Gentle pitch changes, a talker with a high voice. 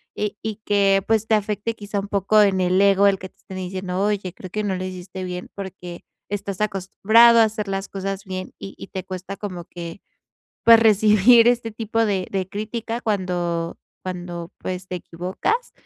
Yes: narrow, 2.3 semitones; high, 195 Hz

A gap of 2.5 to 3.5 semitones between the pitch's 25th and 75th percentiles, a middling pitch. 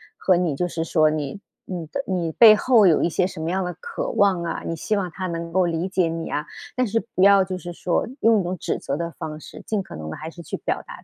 Yes: average, 3.0 semitones; medium, 180 Hz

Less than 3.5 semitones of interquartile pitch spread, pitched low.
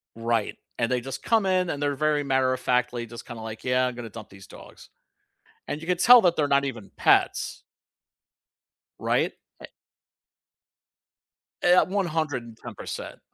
No: average, 5.1 semitones; low, 130 Hz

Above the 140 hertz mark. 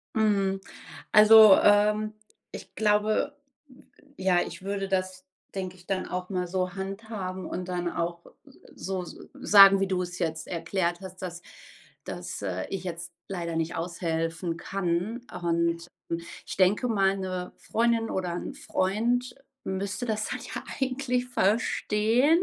Yes: high, 190 Hz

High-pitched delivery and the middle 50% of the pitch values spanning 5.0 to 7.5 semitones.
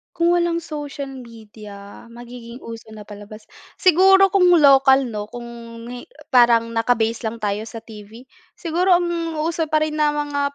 Yes: high, 245 Hz; wide, 5.5 semitones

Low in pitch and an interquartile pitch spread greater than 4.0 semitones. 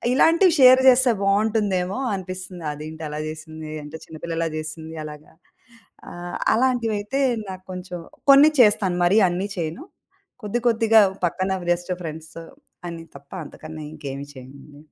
No: medium, 175 Hz; wide, 5.5 semitones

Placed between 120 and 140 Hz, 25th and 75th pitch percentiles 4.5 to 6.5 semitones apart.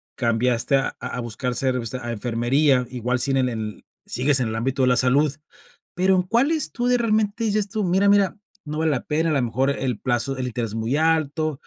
Yes: low, 135 Hz; average, 5.1 semitones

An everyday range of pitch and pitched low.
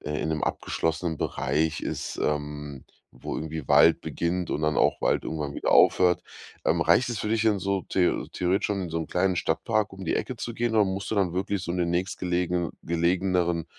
Yes: average, 3.3 semitones; very low, 90 Hz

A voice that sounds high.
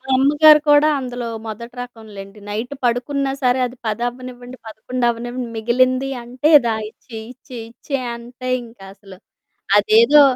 Yes: high, 245 Hz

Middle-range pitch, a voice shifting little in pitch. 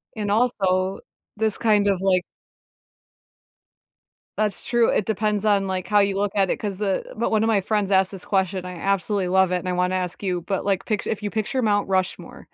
No: high, 195 Hz; narrow, 2.2 semitones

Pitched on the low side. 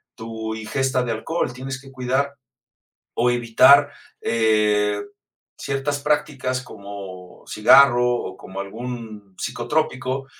Yes: low, 120 Hz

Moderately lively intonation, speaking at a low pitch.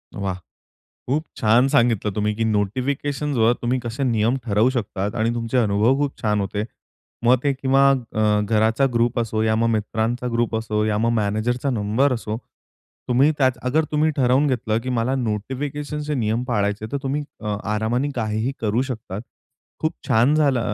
Yes: average, 3.5 semitones; low, 115 Hz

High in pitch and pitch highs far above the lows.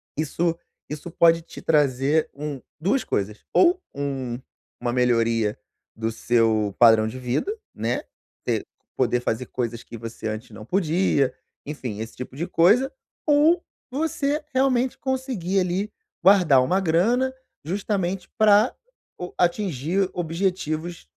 No: medium, 160 Hz; wide, 8.1 semitones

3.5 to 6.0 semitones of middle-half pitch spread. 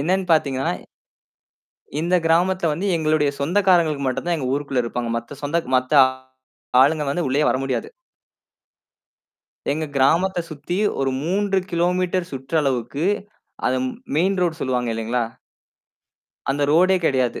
Yes: average, 4.7 semitones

